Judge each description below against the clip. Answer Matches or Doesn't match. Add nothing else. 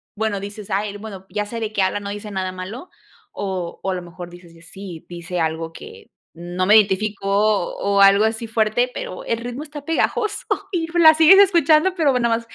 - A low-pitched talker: Doesn't match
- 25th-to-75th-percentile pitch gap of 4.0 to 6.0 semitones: Matches